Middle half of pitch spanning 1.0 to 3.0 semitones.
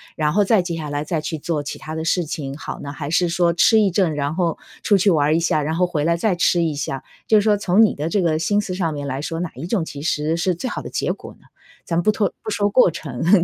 No: average, 3.7 semitones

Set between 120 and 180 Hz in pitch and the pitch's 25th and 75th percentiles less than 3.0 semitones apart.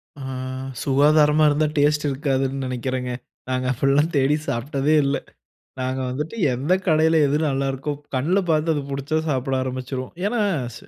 Yes: medium, 140 Hz; narrow, 2.4 semitones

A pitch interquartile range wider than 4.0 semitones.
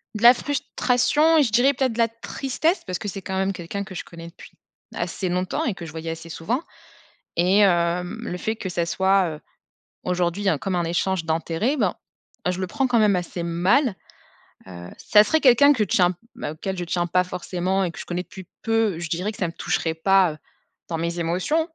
Yes: average, 4.6 semitones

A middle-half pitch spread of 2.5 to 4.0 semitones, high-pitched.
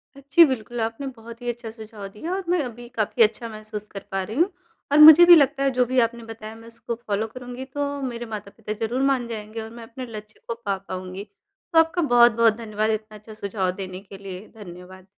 Yes: average, 2.9 semitones; high, 225 Hz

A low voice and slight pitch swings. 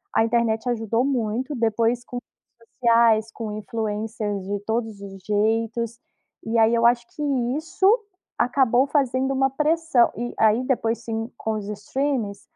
No: high, 230 Hz; narrow, 2.3 semitones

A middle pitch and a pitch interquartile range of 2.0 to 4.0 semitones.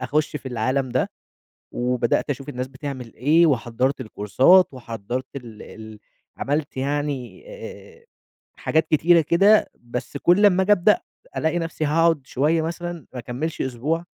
No: medium, 145 Hz; average, 4.8 semitones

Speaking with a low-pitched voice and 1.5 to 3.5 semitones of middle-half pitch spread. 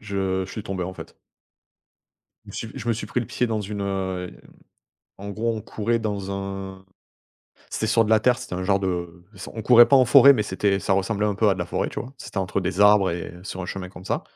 Yes: low, 100 Hz; average, 2.8 semitones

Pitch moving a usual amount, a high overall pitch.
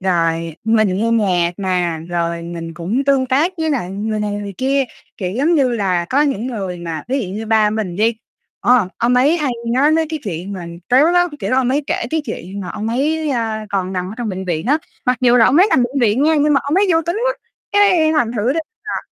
No: wide, 6.8 semitones; high, 230 Hz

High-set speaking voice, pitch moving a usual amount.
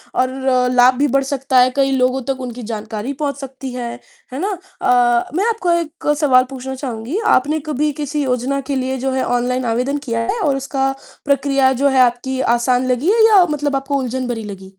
No: very high, 265 Hz; narrow, 2.0 semitones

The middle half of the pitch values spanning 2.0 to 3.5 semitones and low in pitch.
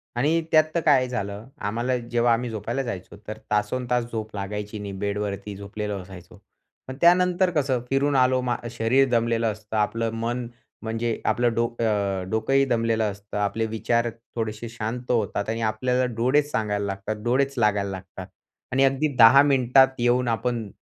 Yes: average, 3.1 semitones; low, 115 Hz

